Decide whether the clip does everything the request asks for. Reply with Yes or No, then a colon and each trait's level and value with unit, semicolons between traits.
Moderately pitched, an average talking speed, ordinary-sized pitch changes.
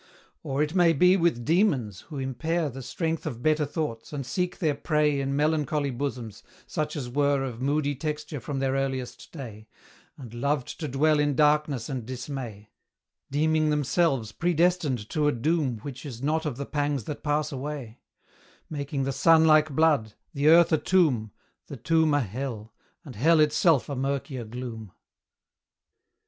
Yes: medium, 145 Hz; average, 165 wpm; average, 3.3 semitones